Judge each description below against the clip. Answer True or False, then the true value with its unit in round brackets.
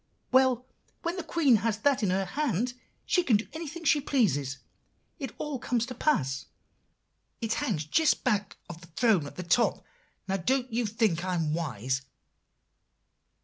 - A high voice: True (225 Hz)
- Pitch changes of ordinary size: False (7.5 semitones)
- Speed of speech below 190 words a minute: True (165 wpm)